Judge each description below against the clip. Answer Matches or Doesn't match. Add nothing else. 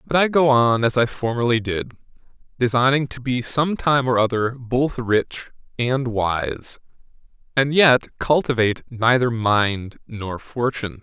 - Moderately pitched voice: Doesn't match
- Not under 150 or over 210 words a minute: Doesn't match